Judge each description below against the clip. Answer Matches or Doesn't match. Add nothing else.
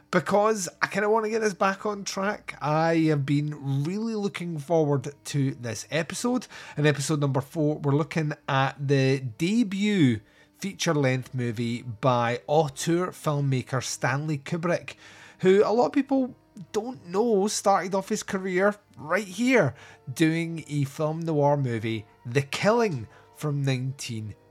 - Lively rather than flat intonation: Matches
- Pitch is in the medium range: Matches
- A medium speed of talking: Matches